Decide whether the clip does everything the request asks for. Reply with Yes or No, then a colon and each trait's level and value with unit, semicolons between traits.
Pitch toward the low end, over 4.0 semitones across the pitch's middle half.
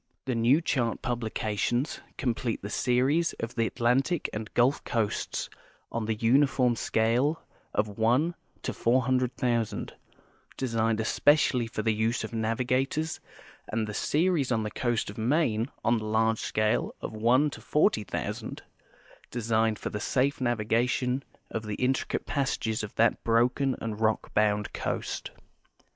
No: low, 120 Hz; average, 2.8 semitones